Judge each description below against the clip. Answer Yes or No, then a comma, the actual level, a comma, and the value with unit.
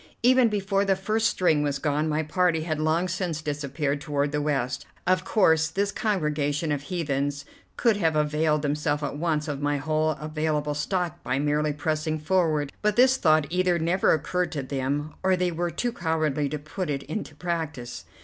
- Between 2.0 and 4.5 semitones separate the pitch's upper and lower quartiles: Yes, average, 3.5 semitones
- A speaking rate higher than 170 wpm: Yes, average, 180 wpm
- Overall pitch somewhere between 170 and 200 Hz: No, medium, 155 Hz